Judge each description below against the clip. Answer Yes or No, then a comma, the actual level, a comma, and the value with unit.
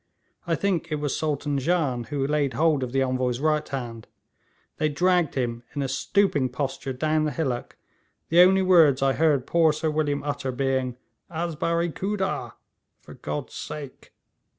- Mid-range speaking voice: Yes, medium, 145 Hz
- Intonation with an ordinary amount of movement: Yes, average, 3.6 semitones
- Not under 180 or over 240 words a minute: No, average, 165 wpm